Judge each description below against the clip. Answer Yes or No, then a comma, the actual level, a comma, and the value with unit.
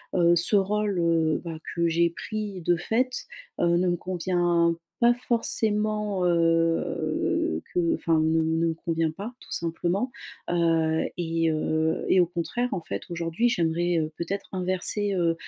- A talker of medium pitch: Yes, medium, 170 Hz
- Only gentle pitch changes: No, average, 3.0 semitones